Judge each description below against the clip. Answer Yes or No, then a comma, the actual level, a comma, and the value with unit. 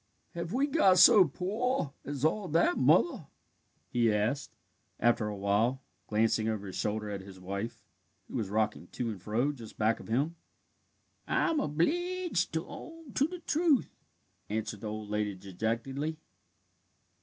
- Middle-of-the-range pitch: No, low, 125 Hz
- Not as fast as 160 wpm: Yes, average, 150 wpm